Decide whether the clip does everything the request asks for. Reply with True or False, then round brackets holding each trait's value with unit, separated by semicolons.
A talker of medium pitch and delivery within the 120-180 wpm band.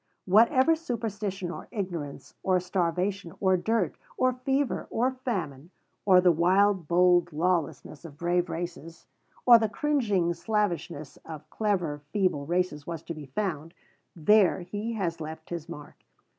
True (180 Hz; 140 wpm)